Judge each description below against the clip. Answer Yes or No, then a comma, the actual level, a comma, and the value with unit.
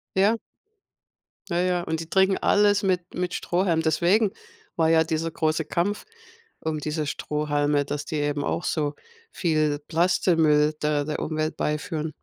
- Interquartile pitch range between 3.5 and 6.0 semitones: No, average, 2.9 semitones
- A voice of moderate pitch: Yes, medium, 160 Hz